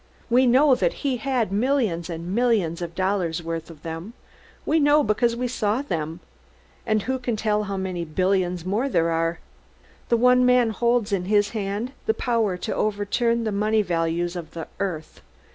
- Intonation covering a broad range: Yes, wide, 5.7 semitones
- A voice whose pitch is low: No, high, 205 Hz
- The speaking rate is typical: Yes, average, 180 wpm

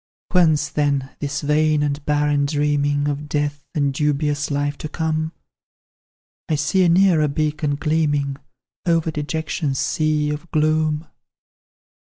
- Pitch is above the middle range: No, medium, 150 Hz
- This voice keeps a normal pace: No, slow, 125 wpm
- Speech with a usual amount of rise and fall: No, narrow, 1.3 semitones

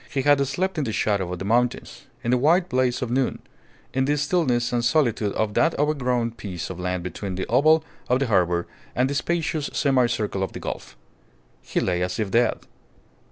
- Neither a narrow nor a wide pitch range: No, wide, 5.8 semitones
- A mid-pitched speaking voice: No, low, 125 Hz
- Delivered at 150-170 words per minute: No, fast, 205 wpm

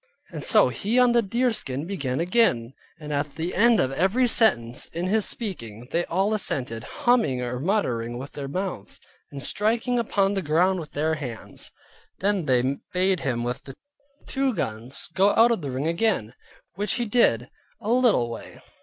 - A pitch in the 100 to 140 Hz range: No, medium, 170 Hz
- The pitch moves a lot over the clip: Yes, wide, 8.9 semitones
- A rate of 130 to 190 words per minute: Yes, average, 175 wpm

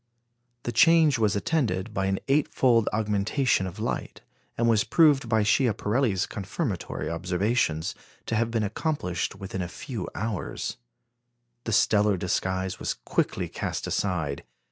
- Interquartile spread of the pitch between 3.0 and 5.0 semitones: Yes, average, 4.2 semitones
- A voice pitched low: Yes, low, 105 Hz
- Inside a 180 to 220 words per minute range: No, slow, 135 wpm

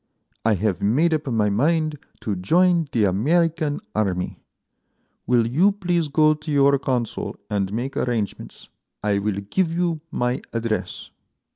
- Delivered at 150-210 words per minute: No, average, 140 wpm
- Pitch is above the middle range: No, low, 130 Hz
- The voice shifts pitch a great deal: Yes, wide, 7.1 semitones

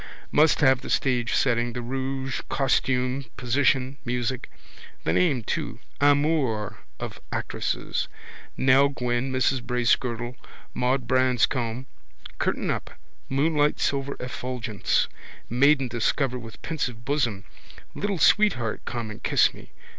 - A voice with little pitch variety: Yes, narrow, 2.3 semitones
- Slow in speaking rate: Yes, slow, 115 wpm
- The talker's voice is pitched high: No, low, 130 Hz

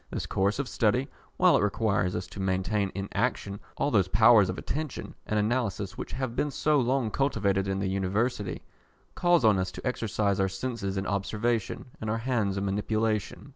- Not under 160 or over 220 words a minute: Yes, average, 185 wpm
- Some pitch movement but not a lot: Yes, average, 3.7 semitones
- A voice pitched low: Yes, low, 105 Hz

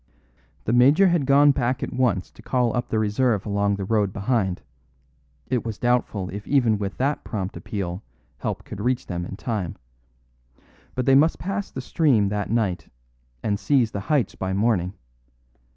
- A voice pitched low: Yes, low, 110 Hz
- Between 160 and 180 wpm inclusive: Yes, average, 170 wpm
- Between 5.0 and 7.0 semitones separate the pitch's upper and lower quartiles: No, average, 4.3 semitones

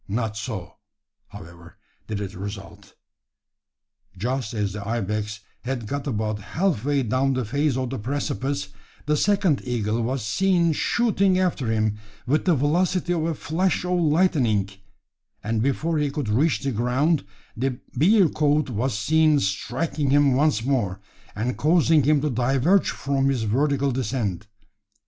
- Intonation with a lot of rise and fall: Yes, wide, 5.7 semitones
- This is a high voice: No, low, 135 Hz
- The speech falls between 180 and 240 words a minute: No, average, 145 wpm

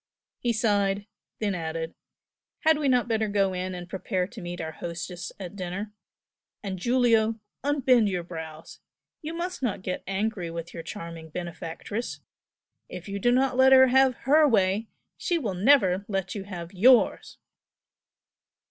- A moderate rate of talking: Yes, average, 155 wpm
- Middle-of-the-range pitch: No, high, 200 Hz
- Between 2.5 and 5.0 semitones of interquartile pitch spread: No, wide, 5.4 semitones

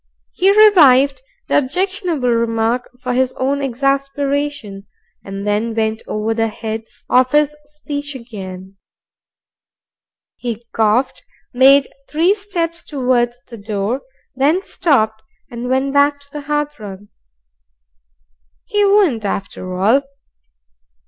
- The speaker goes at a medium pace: No, slow, 110 wpm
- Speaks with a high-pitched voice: Yes, very high, 260 Hz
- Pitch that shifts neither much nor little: Yes, average, 4.7 semitones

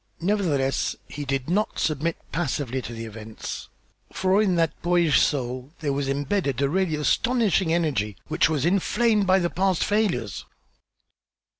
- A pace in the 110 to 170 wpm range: Yes, average, 145 wpm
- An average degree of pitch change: No, wide, 5.7 semitones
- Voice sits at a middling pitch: Yes, medium, 160 Hz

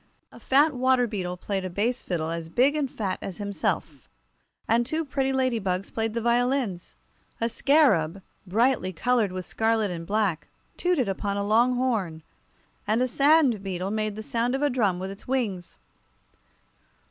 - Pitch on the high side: Yes, high, 220 Hz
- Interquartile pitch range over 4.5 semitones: Yes, average, 5.2 semitones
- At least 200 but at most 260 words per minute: No, average, 165 wpm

